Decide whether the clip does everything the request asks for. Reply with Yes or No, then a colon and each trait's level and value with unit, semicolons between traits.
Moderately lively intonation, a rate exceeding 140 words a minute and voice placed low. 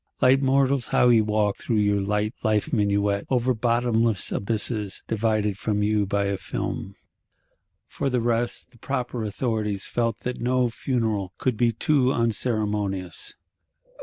No: average, 3.0 semitones; slow, 135 wpm; low, 110 Hz